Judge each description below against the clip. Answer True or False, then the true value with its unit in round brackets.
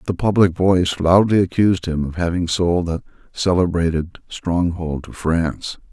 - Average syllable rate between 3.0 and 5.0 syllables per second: True (4.7 syllables/s)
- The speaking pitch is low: True (85 Hz)